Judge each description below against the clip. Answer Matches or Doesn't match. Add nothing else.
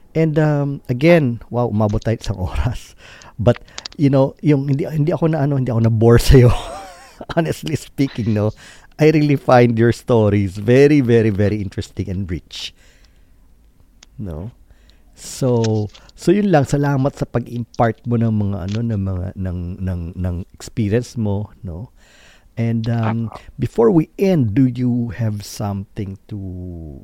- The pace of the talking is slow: Doesn't match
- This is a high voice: Doesn't match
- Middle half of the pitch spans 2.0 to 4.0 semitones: Doesn't match